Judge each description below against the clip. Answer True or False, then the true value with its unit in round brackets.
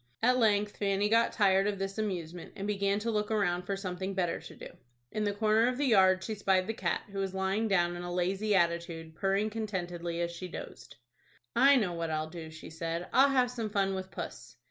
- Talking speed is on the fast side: True (220 wpm)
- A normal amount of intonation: True (3.3 semitones)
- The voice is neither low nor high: False (195 Hz)